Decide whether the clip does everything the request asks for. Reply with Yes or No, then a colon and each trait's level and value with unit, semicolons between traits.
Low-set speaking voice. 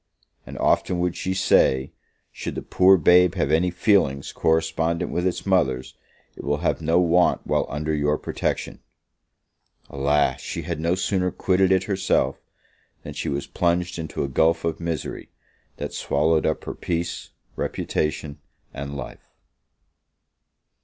Yes: very low, 85 Hz